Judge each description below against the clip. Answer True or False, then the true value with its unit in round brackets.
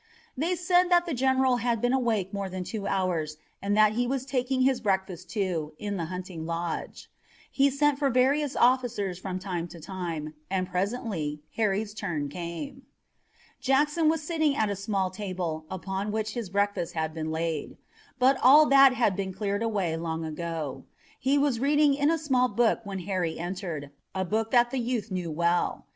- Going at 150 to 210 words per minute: True (180 wpm)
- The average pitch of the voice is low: False (205 Hz)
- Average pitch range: False (6.5 semitones)